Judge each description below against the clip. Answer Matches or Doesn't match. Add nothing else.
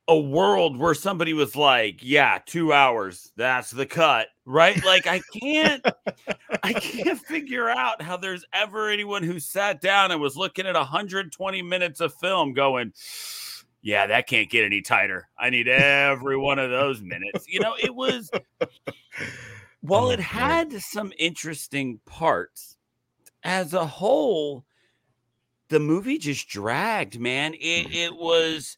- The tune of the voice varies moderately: Doesn't match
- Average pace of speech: Matches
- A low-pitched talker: Doesn't match